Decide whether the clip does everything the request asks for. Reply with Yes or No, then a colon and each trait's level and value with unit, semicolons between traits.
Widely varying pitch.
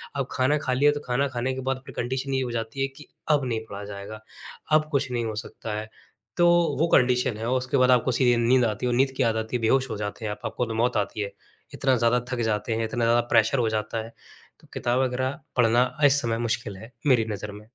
No: average, 2.8 semitones